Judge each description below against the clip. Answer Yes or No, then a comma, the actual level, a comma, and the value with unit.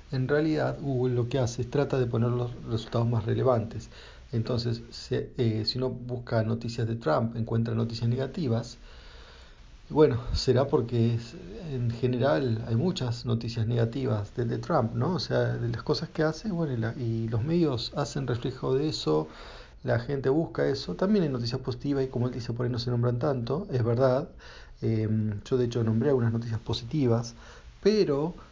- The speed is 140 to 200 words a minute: Yes, average, 180 wpm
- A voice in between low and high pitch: No, low, 120 Hz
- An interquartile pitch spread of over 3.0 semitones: No, average, 2.7 semitones